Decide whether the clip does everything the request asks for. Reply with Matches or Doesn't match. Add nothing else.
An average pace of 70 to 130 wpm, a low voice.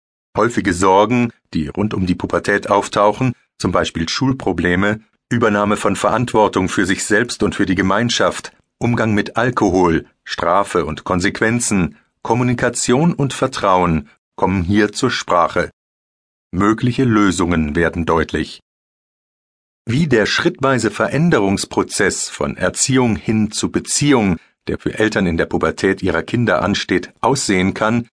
Matches